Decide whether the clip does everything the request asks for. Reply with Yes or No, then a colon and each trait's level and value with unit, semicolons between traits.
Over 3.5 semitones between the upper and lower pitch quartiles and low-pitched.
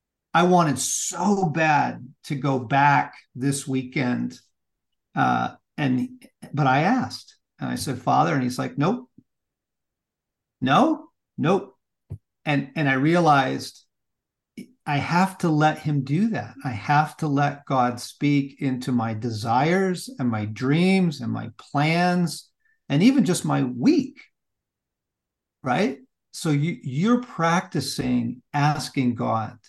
No: wide, 5.4 semitones; medium, 150 Hz